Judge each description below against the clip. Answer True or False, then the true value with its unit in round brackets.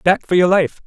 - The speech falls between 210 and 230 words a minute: False (280 wpm)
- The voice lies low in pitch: False (180 Hz)